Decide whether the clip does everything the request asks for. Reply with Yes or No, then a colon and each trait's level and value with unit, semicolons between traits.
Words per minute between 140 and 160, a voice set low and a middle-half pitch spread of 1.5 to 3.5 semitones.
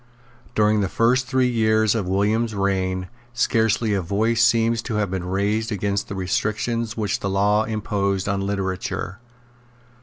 Yes: average, 150 wpm; low, 105 Hz; narrow, 2.4 semitones